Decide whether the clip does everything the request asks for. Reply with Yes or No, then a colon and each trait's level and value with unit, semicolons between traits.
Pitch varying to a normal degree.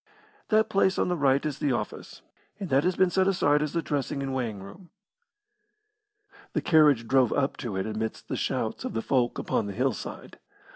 No: wide, 6.1 semitones